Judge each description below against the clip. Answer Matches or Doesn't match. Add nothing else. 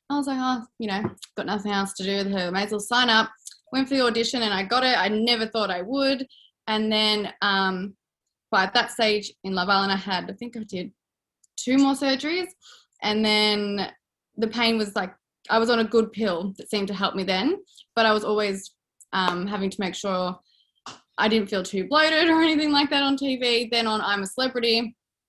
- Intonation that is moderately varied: Matches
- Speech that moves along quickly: Matches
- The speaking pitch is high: Matches